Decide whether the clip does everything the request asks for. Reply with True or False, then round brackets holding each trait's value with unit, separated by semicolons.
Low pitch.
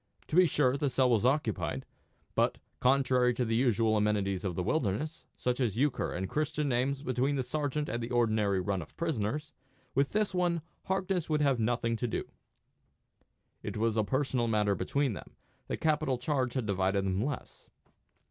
True (125 Hz)